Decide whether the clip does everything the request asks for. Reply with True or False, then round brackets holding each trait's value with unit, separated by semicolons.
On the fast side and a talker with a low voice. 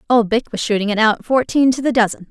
False (260 wpm; 225 Hz)